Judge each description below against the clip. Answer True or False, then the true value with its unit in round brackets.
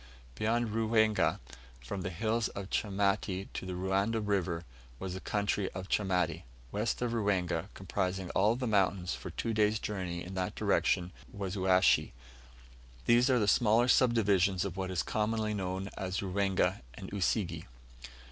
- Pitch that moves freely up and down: False (2.7 semitones)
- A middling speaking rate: True (155 wpm)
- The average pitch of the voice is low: True (100 Hz)